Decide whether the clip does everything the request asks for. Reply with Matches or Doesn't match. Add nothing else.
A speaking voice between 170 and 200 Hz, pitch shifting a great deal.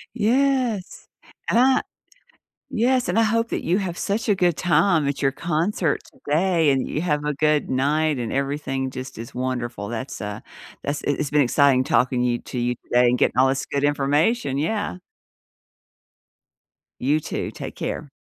Doesn't match